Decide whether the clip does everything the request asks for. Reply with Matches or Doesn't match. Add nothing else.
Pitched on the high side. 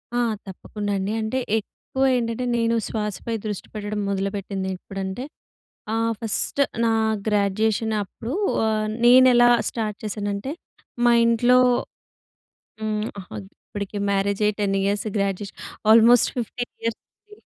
Matches